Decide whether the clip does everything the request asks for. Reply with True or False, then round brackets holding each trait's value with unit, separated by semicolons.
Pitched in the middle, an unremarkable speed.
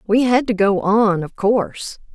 False (210 Hz; 195 wpm)